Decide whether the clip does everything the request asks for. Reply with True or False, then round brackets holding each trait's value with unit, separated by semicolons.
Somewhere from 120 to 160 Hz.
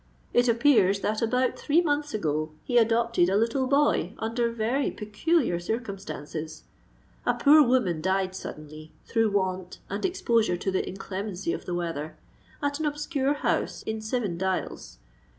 False (220 Hz)